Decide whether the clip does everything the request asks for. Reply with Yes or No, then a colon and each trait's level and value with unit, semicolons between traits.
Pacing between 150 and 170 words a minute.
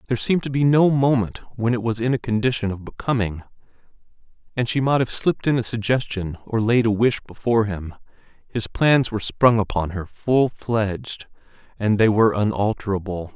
No: average, 180 wpm